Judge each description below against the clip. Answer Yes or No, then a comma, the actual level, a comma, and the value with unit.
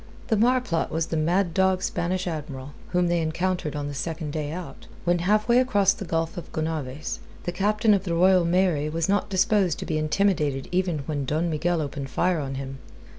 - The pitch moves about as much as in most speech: Yes, average, 3.5 semitones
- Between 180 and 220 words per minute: Yes, average, 195 wpm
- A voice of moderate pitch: Yes, medium, 170 Hz